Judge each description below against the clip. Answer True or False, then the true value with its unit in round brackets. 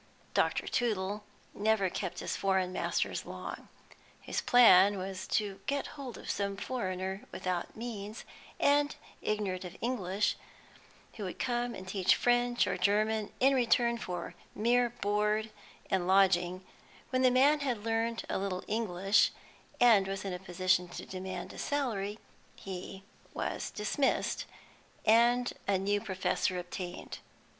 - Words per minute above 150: False (135 wpm)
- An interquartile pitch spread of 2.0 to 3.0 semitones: False (4.0 semitones)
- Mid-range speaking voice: False (205 Hz)